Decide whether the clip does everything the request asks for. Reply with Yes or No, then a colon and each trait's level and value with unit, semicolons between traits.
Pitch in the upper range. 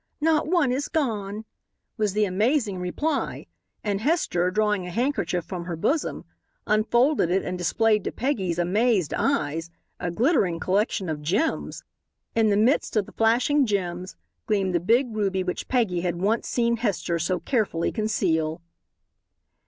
Yes: high, 205 Hz